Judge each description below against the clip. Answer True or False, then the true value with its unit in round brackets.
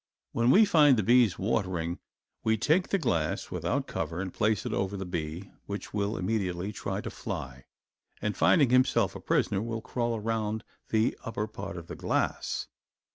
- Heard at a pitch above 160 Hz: False (105 Hz)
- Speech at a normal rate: True (175 wpm)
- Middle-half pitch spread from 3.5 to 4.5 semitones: True (3.9 semitones)